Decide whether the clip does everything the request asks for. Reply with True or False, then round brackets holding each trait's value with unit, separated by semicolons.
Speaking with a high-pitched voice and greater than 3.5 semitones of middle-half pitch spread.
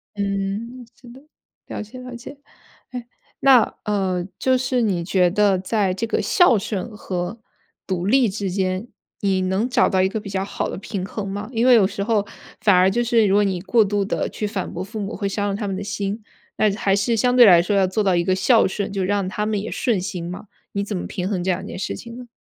False (200 Hz; 3.1 semitones)